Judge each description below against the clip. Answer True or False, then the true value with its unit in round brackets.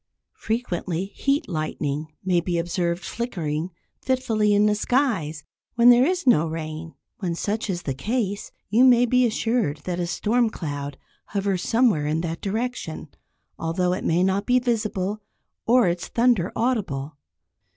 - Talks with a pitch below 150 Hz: False (195 Hz)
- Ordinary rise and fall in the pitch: False (6.2 semitones)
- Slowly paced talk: False (150 wpm)